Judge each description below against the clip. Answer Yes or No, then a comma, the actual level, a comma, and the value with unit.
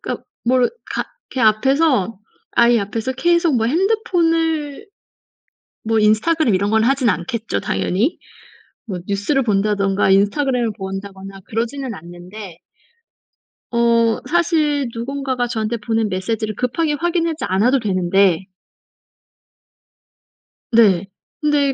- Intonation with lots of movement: Yes, wide, 5.8 semitones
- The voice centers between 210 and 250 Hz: Yes, high, 230 Hz